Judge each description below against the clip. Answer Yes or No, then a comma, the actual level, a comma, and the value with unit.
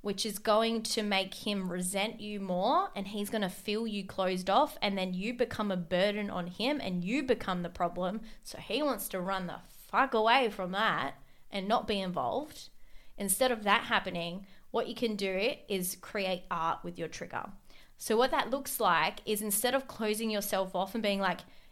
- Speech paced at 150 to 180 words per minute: No, average, 195 wpm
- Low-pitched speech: No, high, 205 Hz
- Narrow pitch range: No, average, 3.3 semitones